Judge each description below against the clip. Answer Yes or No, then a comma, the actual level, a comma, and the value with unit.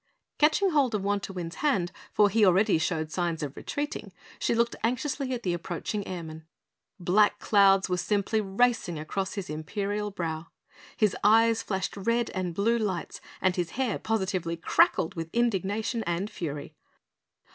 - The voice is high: Yes, high, 195 Hz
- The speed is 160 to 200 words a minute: No, average, 150 wpm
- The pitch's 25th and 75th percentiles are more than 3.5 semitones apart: Yes, average, 4.4 semitones